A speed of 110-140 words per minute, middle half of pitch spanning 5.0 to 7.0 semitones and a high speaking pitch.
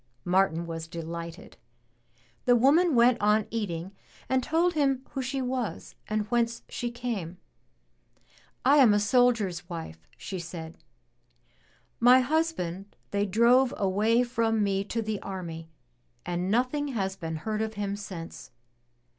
Yes: slow, 135 wpm; wide, 5.6 semitones; high, 215 Hz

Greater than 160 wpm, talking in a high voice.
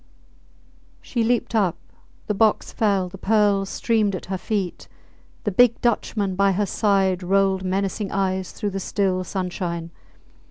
No: average, 145 wpm; high, 195 Hz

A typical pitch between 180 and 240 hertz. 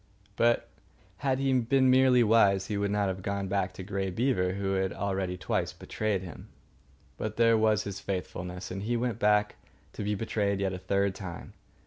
No: low, 100 Hz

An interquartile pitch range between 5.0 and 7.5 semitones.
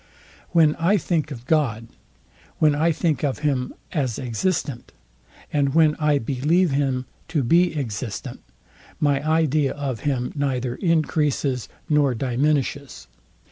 No: average, 3.3 semitones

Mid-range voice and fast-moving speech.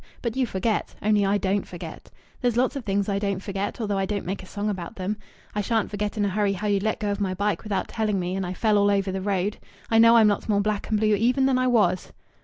No: high, 205 Hz; fast, 275 wpm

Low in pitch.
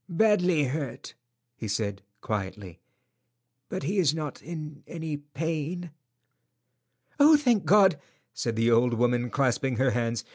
No: medium, 145 Hz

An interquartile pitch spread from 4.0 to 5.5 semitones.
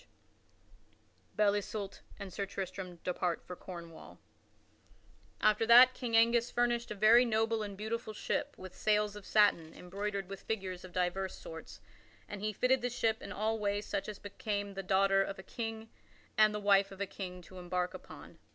No: narrow, 2.6 semitones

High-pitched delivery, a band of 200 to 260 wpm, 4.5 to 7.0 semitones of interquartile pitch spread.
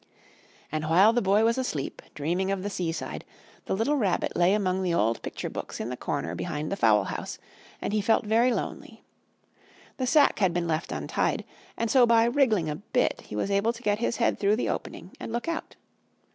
Yes: high, 200 Hz; fast, 205 wpm; wide, 5.4 semitones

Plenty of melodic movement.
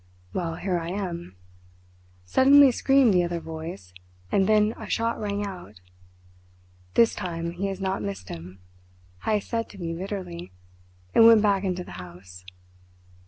No: average, 3.8 semitones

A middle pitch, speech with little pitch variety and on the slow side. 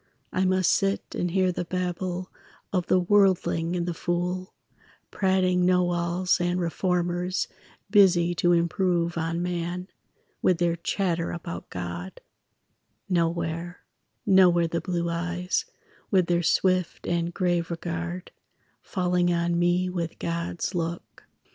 Yes: medium, 175 Hz; narrow, 1.2 semitones; slow, 125 wpm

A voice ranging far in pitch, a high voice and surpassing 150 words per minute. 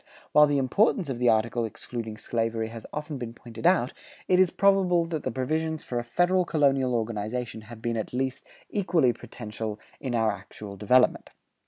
No: wide, 5.7 semitones; low, 125 Hz; average, 180 wpm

